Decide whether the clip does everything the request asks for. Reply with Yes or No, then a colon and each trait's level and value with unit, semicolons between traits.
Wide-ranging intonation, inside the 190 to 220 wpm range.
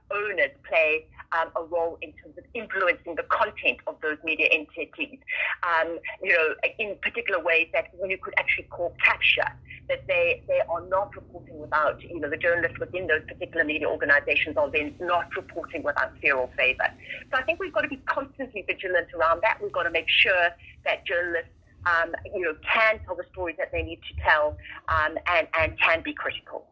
Yes: wide, 8.4 semitones; average, 200 wpm